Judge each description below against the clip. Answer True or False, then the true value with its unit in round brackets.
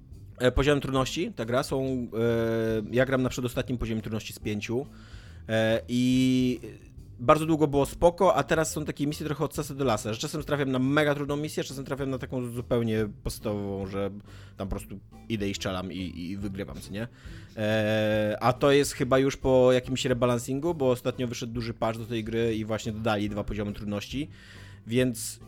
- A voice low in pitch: True (115 Hz)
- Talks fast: True (180 wpm)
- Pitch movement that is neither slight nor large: True (3.7 semitones)